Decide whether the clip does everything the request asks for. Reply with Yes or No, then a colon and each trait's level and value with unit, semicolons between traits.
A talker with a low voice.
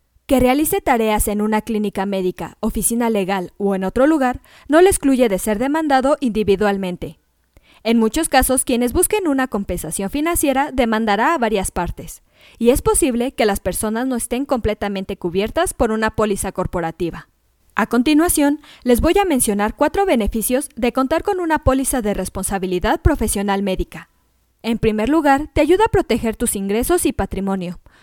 No: high, 230 Hz